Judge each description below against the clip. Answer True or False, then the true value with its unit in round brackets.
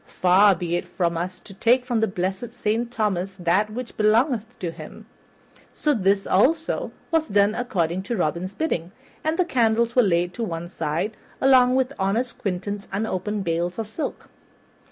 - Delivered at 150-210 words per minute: True (170 wpm)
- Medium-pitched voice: False (205 Hz)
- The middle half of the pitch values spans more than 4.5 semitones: True (4.9 semitones)